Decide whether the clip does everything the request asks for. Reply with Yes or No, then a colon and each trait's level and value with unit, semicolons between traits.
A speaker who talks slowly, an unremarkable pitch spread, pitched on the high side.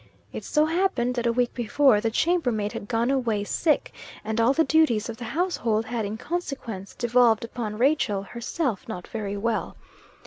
No: average, 175 wpm; average, 3.9 semitones; high, 235 Hz